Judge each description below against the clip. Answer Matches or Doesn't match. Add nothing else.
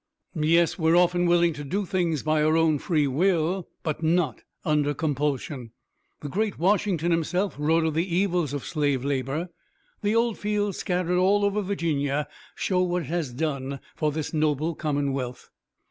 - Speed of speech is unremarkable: Matches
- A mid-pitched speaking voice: Matches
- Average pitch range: Matches